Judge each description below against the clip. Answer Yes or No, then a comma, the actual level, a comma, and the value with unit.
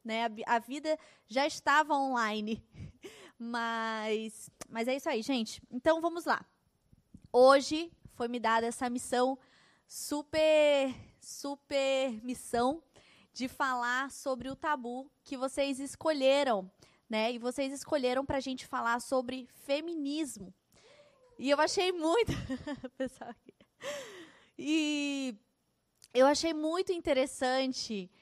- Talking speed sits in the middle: No, slow, 105 wpm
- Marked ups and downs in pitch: No, average, 3.5 semitones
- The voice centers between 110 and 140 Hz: No, very high, 265 Hz